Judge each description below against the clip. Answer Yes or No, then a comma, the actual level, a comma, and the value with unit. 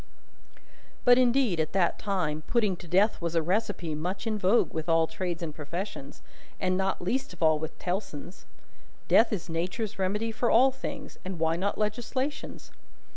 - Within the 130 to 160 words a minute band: No, average, 170 wpm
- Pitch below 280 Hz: Yes, high, 190 Hz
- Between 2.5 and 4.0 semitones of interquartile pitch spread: No, average, 4.9 semitones